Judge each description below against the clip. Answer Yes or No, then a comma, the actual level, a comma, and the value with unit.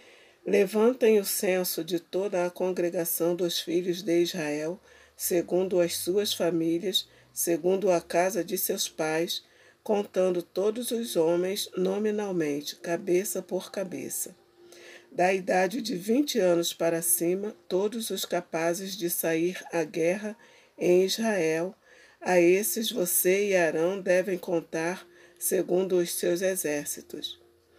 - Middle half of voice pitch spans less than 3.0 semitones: Yes, narrow, 2.4 semitones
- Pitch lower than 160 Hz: No, medium, 180 Hz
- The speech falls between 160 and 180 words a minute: No, slow, 120 wpm